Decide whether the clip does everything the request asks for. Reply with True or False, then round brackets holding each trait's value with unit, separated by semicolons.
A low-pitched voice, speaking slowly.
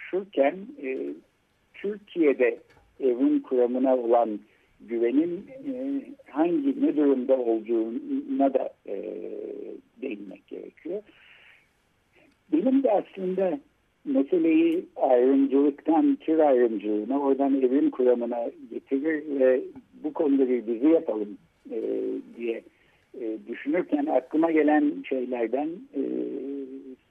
False (150 Hz; 75 wpm)